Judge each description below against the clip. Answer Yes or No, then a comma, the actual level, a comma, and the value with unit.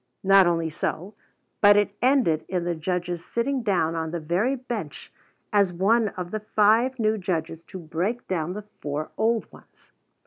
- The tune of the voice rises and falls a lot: No, average, 4.5 semitones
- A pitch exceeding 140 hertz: Yes, high, 190 Hz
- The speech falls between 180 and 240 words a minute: No, average, 170 wpm